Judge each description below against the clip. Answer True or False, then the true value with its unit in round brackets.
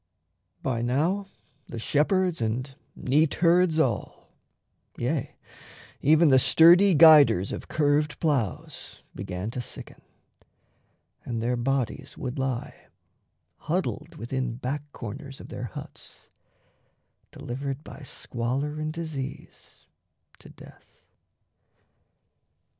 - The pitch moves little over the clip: False (4.1 semitones)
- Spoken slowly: True (95 wpm)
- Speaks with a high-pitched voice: False (135 Hz)